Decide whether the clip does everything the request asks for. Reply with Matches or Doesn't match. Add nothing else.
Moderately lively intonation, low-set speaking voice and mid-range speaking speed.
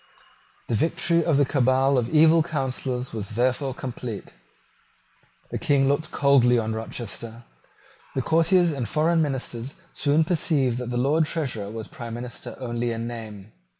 Matches